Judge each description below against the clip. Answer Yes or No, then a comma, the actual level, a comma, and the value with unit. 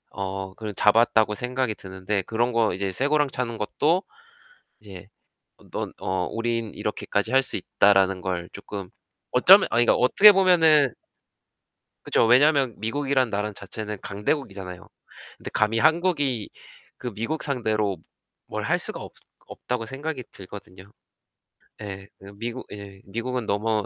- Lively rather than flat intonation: No, average, 4.6 semitones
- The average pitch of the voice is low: Yes, low, 110 Hz